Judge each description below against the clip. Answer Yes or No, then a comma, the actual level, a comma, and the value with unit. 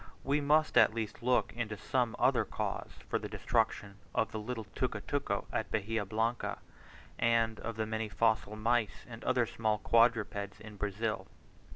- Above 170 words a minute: No, average, 160 wpm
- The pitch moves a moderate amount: No, narrow, 1.6 semitones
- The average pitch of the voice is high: No, low, 110 Hz